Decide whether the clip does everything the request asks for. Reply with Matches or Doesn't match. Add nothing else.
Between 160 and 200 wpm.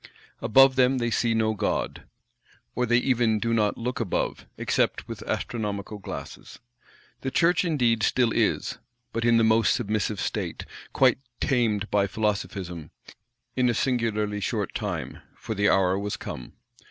Doesn't match